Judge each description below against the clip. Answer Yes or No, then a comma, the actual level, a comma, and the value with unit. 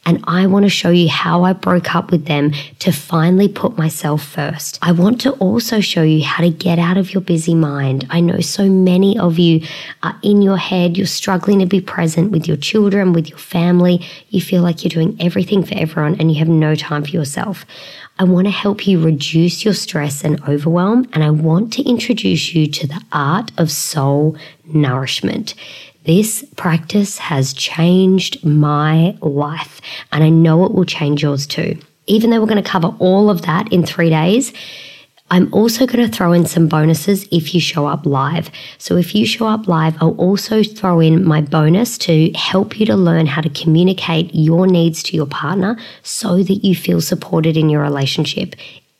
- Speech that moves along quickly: No, average, 195 wpm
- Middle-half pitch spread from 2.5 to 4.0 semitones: Yes, average, 3.4 semitones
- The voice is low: No, medium, 170 Hz